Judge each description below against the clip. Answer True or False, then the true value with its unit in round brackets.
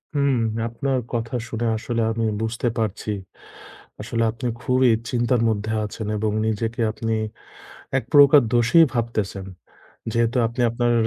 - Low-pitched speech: True (115 Hz)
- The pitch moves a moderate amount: False (1.8 semitones)